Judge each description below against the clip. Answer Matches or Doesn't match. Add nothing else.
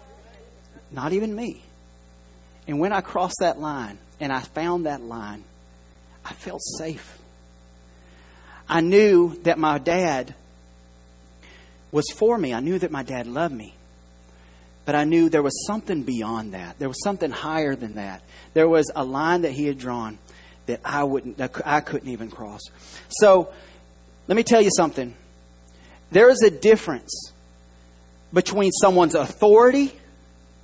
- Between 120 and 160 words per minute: Matches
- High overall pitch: Doesn't match